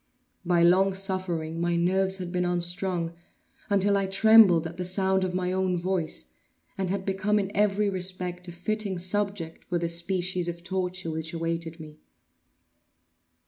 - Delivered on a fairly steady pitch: Yes, narrow, 1.9 semitones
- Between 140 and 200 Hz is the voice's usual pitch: Yes, medium, 185 Hz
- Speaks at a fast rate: No, average, 155 wpm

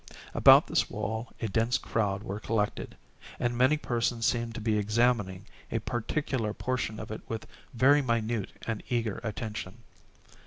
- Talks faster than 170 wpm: No, average, 150 wpm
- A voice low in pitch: Yes, low, 115 Hz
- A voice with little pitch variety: Yes, narrow, 2.1 semitones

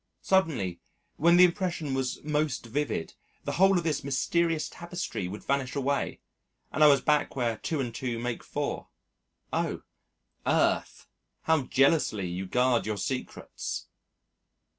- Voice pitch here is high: No, medium, 140 Hz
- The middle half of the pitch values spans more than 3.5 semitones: Yes, average, 4.9 semitones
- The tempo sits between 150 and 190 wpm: No, average, 140 wpm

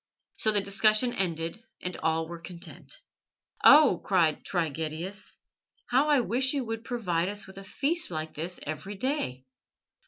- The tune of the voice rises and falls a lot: Yes, wide, 6.1 semitones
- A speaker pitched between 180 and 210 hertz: Yes, high, 190 Hz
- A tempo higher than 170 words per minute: No, average, 150 wpm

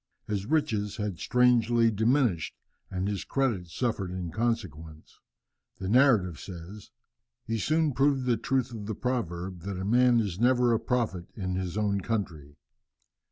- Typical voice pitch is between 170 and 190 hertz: No, low, 105 Hz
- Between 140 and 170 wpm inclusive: Yes, average, 150 wpm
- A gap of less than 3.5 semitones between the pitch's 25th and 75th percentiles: No, average, 4.8 semitones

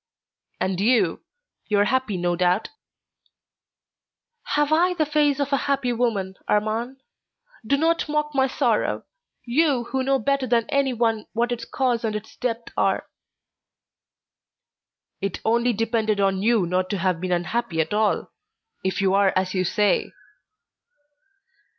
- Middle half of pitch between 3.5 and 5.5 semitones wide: Yes, average, 5.2 semitones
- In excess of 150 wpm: No, average, 145 wpm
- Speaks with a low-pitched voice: No, high, 230 Hz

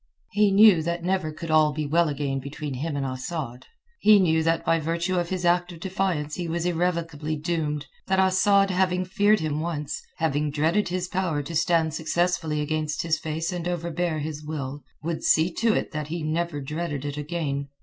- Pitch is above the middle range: No, medium, 165 Hz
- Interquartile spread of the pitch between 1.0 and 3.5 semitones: Yes, average, 2.8 semitones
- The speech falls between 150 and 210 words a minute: Yes, average, 190 wpm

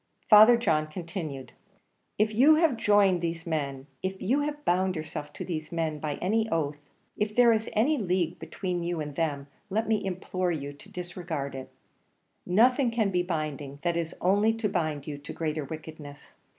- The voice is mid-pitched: Yes, medium, 175 Hz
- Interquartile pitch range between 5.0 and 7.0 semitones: Yes, wide, 5.4 semitones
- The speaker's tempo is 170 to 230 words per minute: Yes, average, 175 wpm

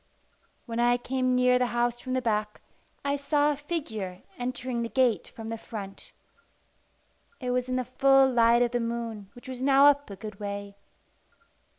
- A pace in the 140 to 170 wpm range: No, average, 180 wpm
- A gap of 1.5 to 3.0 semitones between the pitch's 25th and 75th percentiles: Yes, narrow, 2.4 semitones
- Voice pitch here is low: No, high, 245 Hz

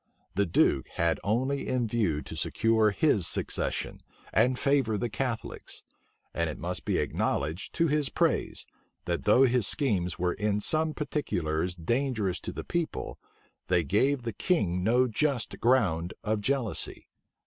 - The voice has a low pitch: Yes, low, 110 Hz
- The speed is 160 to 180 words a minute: No, average, 150 wpm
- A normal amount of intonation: No, wide, 6.6 semitones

